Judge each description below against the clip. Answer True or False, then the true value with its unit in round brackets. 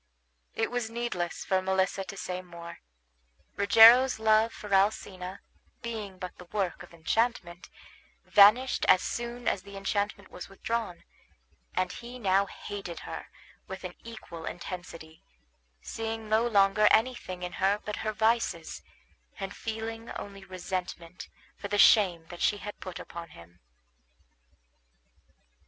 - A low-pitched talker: False (200 Hz)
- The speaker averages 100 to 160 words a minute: True (135 wpm)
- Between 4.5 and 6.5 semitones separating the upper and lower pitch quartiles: False (3.5 semitones)